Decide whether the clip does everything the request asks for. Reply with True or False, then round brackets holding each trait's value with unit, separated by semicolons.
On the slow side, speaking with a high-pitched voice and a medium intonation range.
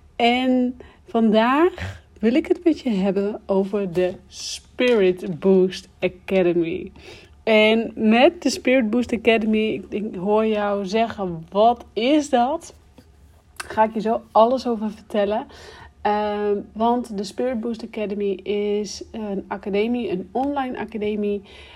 True (125 wpm; 215 Hz; 3.0 semitones)